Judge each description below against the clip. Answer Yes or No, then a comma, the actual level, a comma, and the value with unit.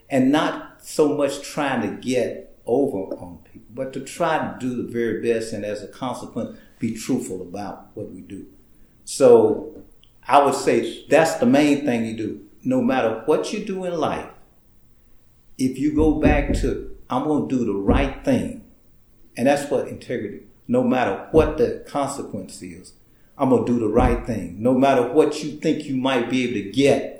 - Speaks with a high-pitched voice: No, medium, 140 Hz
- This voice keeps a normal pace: Yes, average, 185 wpm